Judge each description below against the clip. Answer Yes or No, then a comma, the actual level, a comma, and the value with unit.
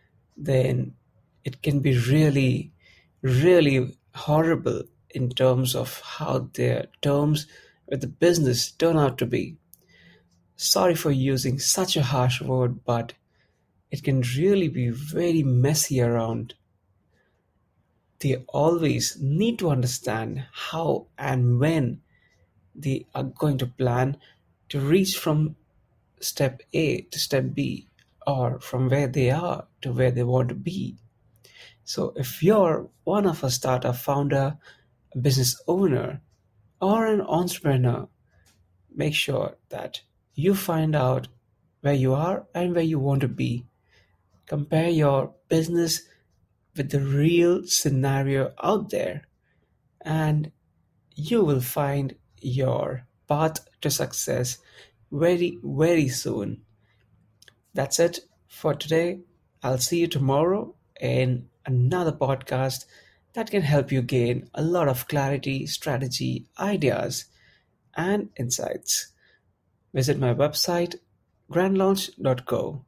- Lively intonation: No, average, 4.3 semitones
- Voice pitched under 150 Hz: Yes, low, 135 Hz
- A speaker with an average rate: No, slow, 120 wpm